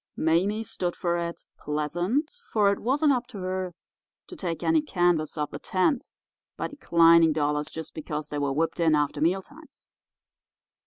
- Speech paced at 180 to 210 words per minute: No, average, 165 wpm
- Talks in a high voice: No, medium, 175 Hz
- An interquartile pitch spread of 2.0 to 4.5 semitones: No, wide, 5.4 semitones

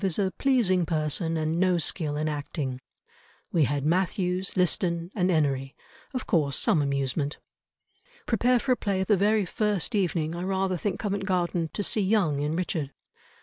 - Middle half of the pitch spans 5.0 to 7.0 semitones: No, average, 4.0 semitones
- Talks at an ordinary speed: Yes, average, 165 wpm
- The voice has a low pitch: No, medium, 180 Hz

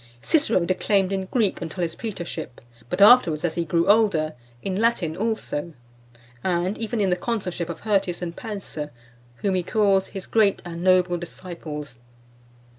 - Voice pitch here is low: No, medium, 185 Hz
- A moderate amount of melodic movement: Yes, average, 3.3 semitones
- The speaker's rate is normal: Yes, average, 155 wpm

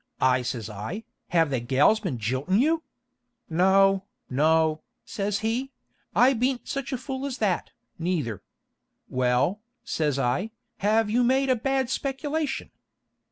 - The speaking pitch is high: Yes, high, 195 Hz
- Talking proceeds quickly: No, slow, 135 wpm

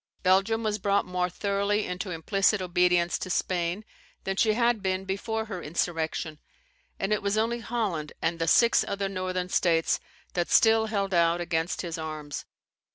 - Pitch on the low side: No, medium, 185 Hz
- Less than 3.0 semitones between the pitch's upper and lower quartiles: No, average, 3.4 semitones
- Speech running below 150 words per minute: No, average, 160 wpm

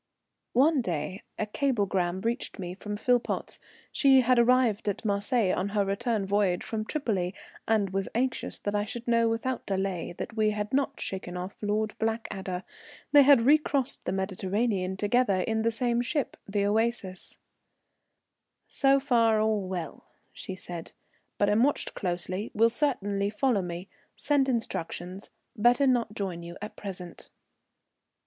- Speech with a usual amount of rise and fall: Yes, average, 4.0 semitones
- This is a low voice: No, high, 210 Hz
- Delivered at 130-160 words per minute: Yes, average, 150 wpm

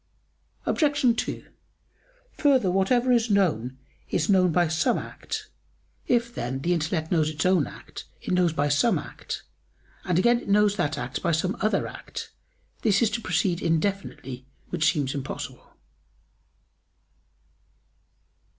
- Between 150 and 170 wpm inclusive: No, average, 140 wpm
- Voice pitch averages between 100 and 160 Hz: No, medium, 180 Hz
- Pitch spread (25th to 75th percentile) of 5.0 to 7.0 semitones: Yes, wide, 5.4 semitones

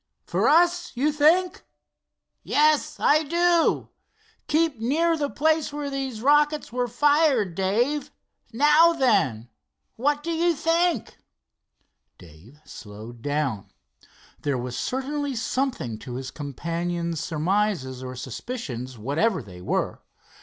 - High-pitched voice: Yes, high, 245 Hz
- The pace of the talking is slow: Yes, slow, 115 wpm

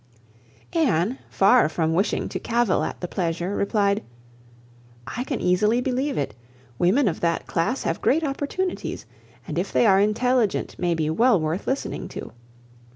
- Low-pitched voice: No, high, 205 Hz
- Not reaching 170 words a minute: Yes, average, 155 wpm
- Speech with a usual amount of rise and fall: No, wide, 6.4 semitones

